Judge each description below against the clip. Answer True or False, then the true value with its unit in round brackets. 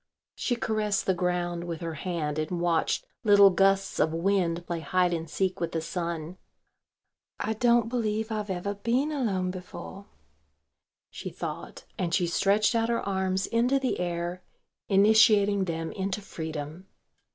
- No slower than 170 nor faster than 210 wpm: False (150 wpm)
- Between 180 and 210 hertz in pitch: True (190 Hz)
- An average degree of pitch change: True (3.5 semitones)